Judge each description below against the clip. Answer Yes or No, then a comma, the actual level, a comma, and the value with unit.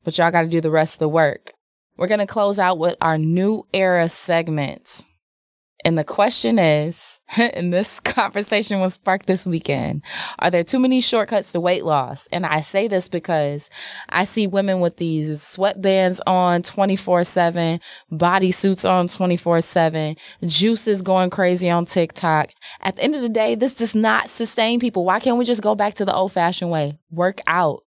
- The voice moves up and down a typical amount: Yes, average, 3.4 semitones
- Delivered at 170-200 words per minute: Yes, average, 180 wpm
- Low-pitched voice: No, medium, 180 Hz